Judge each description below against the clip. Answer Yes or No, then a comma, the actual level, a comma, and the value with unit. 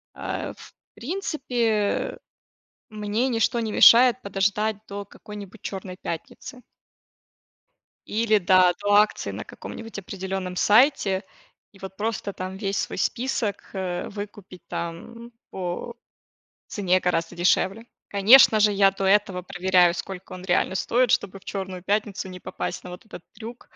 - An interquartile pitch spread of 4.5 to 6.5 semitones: No, average, 2.9 semitones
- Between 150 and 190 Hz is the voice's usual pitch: No, high, 200 Hz